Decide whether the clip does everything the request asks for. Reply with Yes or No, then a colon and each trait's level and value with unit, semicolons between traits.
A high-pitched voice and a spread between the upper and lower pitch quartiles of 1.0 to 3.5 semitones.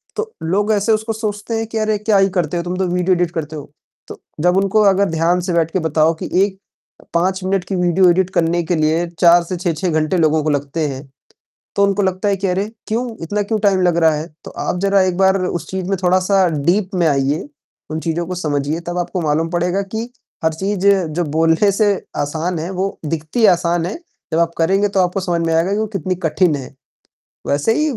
No: medium, 180 Hz; average, 3.2 semitones